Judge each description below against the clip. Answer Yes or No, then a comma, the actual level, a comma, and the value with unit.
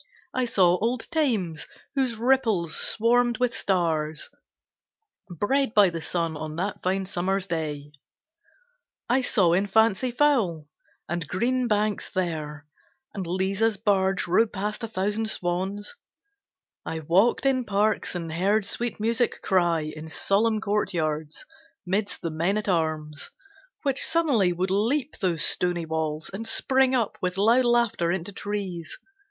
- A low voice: No, high, 195 Hz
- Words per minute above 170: No, slow, 135 wpm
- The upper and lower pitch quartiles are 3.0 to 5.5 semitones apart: Yes, average, 5.0 semitones